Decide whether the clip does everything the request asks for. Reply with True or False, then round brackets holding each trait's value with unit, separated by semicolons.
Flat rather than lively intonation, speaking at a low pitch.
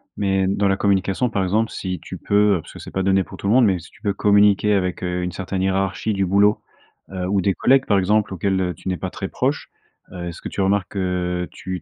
True (1.8 semitones; 95 Hz)